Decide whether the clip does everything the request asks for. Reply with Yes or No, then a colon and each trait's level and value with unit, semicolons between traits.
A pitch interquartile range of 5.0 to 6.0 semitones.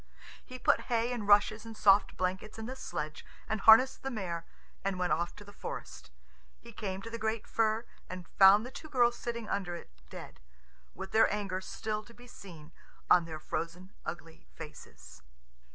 No: average, 4.2 semitones